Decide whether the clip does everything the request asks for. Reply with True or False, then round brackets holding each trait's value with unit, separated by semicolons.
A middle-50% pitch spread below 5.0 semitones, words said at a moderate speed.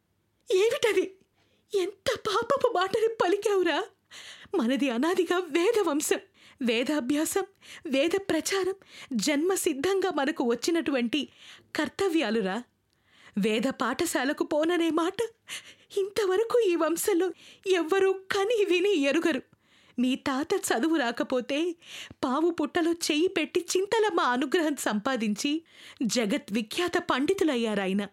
False (5.4 semitones; 85 wpm)